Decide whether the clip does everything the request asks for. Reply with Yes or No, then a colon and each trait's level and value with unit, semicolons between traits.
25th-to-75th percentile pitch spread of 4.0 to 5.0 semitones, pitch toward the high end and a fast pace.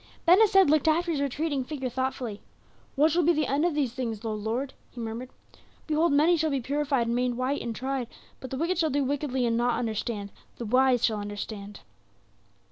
Yes: average, 4.3 semitones; very high, 265 Hz; fast, 210 wpm